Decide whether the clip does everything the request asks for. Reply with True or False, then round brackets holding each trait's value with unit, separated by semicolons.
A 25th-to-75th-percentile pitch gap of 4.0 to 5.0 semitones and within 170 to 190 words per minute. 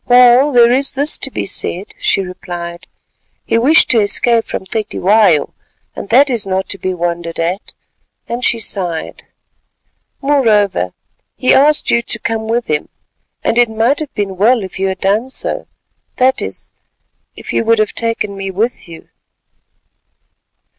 False (4.4 semitones; 160 wpm)